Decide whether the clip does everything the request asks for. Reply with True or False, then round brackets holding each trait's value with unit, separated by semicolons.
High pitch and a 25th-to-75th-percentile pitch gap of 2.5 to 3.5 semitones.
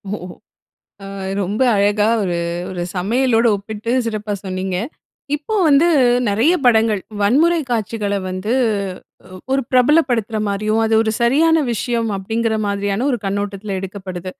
True (215 Hz; 3.2 semitones)